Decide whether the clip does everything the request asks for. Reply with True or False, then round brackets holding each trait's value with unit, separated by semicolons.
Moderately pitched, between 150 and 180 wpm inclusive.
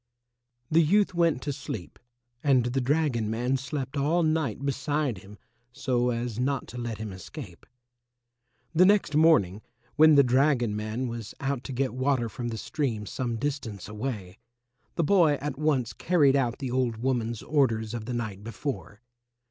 False (130 Hz; 165 wpm)